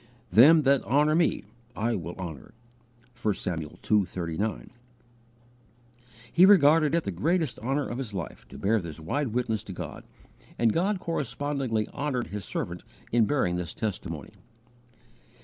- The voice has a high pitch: No, low, 115 Hz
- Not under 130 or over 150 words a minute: Yes, average, 145 wpm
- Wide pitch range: Yes, wide, 7.2 semitones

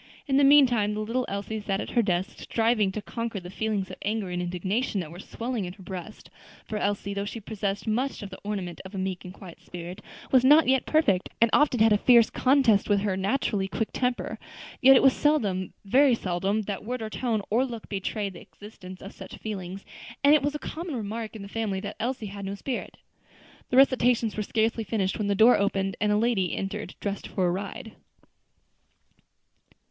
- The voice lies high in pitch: Yes, high, 210 Hz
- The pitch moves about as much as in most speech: Yes, average, 3.6 semitones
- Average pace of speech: No, fast, 210 wpm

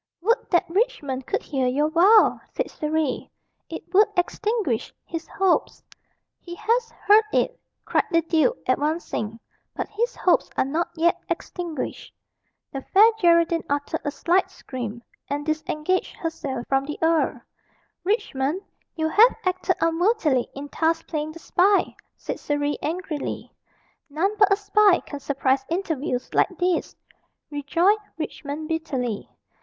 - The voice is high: Yes, very high, 330 Hz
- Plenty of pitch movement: No, average, 4.7 semitones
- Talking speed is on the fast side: No, slow, 135 wpm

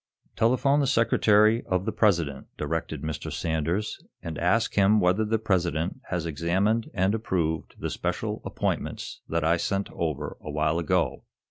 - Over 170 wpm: No, average, 150 wpm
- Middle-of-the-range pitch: No, very low, 90 Hz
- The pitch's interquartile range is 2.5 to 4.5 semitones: No, average, 4.9 semitones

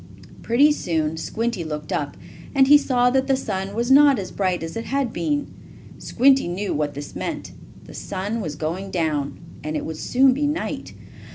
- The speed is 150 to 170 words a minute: No, average, 185 wpm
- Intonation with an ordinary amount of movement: No, wide, 8.7 semitones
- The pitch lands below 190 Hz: No, high, 205 Hz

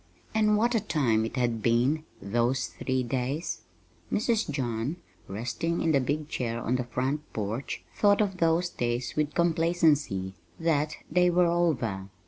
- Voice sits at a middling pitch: Yes, medium, 145 Hz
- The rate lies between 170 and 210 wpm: No, average, 150 wpm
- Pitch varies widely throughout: Yes, wide, 6.1 semitones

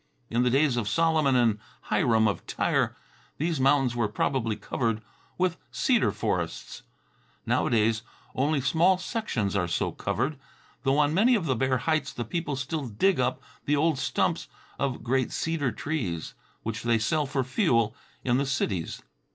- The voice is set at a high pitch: No, low, 130 Hz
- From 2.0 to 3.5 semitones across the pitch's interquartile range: No, average, 5.2 semitones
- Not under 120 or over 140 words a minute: No, average, 160 wpm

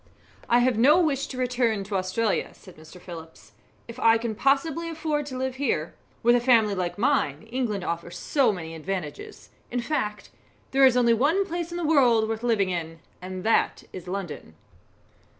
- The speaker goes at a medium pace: Yes, average, 180 wpm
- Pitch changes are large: Yes, wide, 6.5 semitones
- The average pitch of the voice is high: Yes, high, 230 Hz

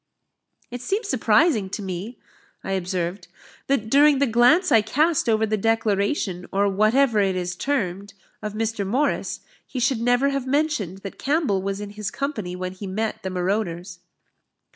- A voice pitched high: Yes, high, 215 Hz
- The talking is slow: No, average, 165 wpm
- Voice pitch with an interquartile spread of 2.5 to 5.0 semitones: No, wide, 5.5 semitones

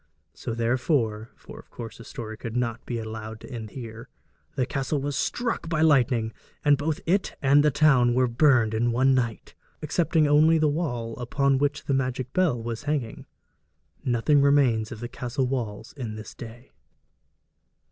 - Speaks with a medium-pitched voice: No, low, 125 Hz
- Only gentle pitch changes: No, average, 3.9 semitones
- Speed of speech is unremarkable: Yes, average, 170 wpm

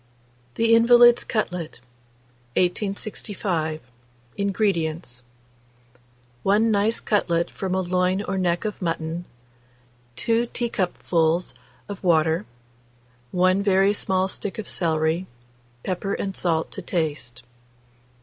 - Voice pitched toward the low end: No, medium, 185 Hz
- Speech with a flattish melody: No, average, 3.5 semitones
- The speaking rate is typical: No, slow, 100 wpm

